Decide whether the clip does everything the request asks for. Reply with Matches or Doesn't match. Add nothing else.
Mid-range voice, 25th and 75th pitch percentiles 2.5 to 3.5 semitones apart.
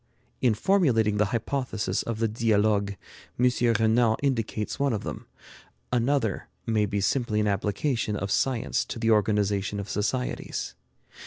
Doesn't match